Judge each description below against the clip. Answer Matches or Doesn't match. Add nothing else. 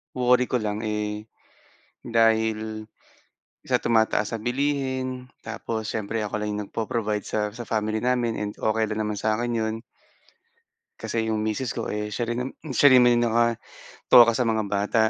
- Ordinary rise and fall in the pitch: Doesn't match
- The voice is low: Matches